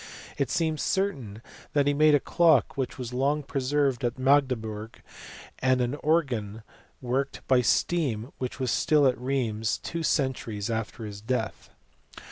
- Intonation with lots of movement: No, average, 4.0 semitones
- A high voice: No, low, 130 Hz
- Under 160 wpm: Yes, average, 145 wpm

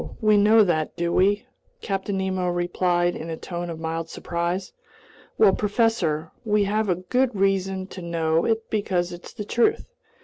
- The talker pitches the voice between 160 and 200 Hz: Yes, high, 190 Hz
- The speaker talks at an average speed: Yes, average, 160 wpm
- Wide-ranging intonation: No, average, 3.4 semitones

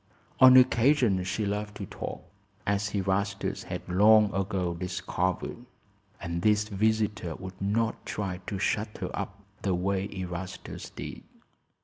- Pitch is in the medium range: No, low, 100 Hz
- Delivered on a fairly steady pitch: Yes, narrow, 2.3 semitones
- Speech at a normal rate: No, slow, 130 wpm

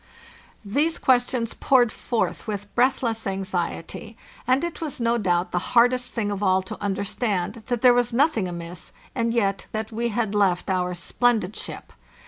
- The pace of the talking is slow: No, average, 160 wpm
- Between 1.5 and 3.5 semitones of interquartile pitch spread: No, average, 4.1 semitones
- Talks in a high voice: Yes, high, 220 Hz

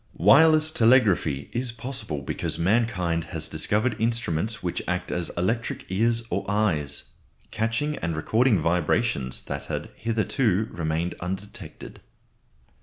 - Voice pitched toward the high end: No, low, 105 Hz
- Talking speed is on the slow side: Yes, slow, 115 wpm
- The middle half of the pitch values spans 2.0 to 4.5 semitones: No, average, 5.3 semitones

